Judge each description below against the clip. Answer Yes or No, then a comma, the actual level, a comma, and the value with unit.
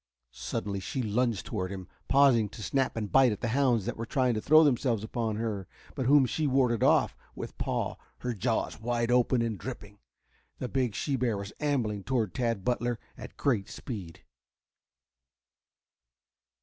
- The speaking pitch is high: No, low, 120 Hz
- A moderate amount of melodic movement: Yes, average, 3.4 semitones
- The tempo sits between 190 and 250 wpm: No, average, 165 wpm